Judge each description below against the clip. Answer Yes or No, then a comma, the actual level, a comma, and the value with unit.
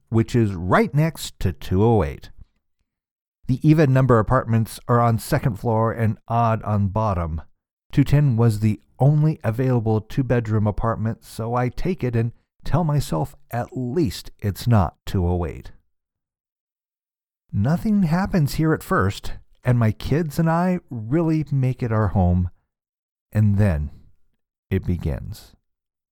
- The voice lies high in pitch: No, low, 115 Hz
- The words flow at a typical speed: No, slow, 130 wpm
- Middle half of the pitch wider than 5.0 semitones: Yes, wide, 5.6 semitones